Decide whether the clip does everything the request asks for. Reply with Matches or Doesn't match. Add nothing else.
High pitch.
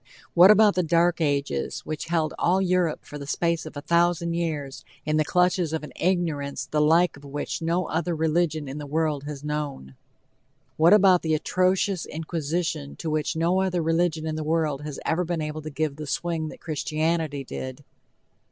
Doesn't match